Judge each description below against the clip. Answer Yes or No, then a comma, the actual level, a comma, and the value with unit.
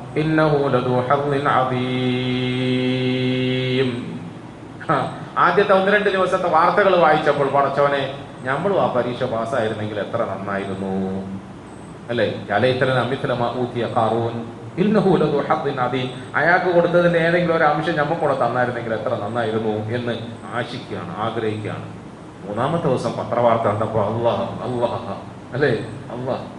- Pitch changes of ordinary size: Yes, average, 4.0 semitones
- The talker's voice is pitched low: Yes, low, 125 Hz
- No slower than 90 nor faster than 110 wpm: No, average, 75 wpm